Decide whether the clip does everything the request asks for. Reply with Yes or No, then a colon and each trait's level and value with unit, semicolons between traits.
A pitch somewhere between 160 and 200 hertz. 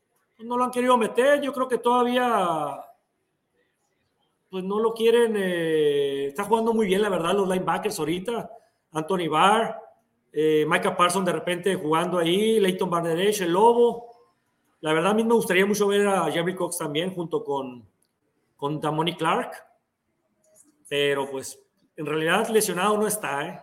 Yes: high, 190 Hz